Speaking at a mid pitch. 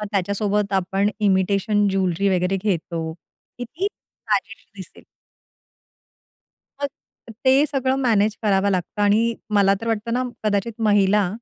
No: high, 205 Hz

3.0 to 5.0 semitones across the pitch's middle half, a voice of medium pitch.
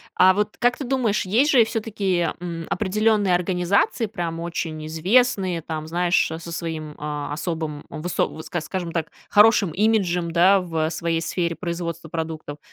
Yes: average, 3.6 semitones; medium, 175 Hz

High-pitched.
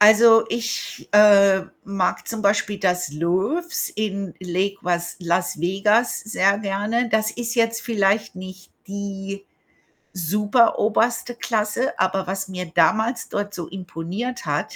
Yes: high, 200 Hz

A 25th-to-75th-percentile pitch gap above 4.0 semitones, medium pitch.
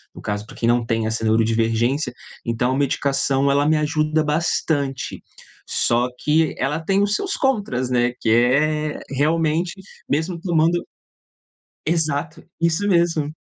Yes: average, 4.9 semitones; medium, 150 Hz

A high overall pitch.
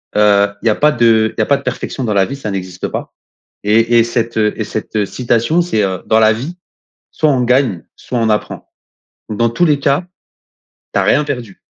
No: low, 115 Hz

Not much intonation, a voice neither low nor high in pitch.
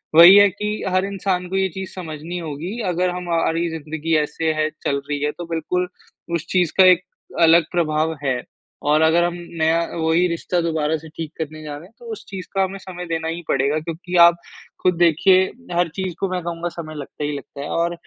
Yes: narrow, 2.3 semitones; medium, 170 Hz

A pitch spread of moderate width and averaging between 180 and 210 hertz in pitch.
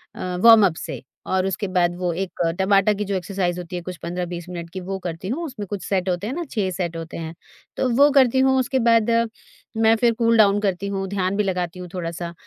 Yes: average, 3.4 semitones; high, 190 Hz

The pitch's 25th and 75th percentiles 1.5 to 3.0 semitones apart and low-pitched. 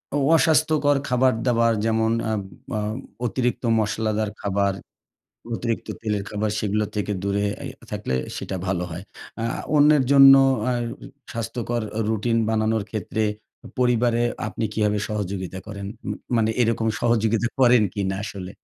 Yes: narrow, 2.6 semitones; low, 110 Hz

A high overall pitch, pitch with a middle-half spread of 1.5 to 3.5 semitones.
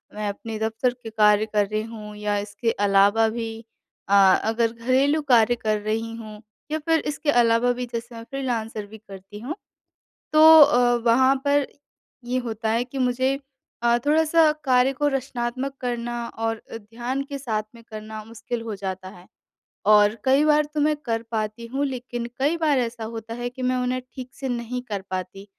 Yes: high, 235 Hz; average, 3.1 semitones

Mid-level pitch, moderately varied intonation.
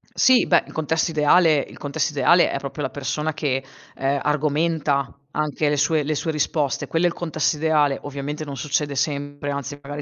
No: medium, 150 Hz; narrow, 1.9 semitones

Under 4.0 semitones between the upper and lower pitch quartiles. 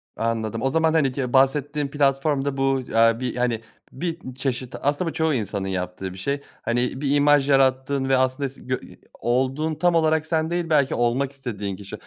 Yes: average, 3.1 semitones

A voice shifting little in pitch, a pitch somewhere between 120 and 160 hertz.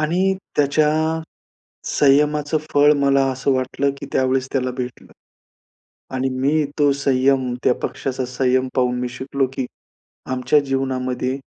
Yes: narrow, 1.7 semitones; low, 135 Hz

